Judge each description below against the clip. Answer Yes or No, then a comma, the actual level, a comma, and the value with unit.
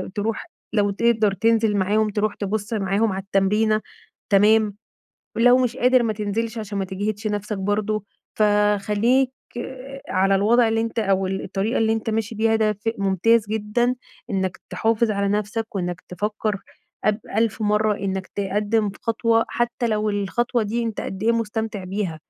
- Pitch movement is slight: Yes, narrow, 2.0 semitones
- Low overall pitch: No, high, 215 Hz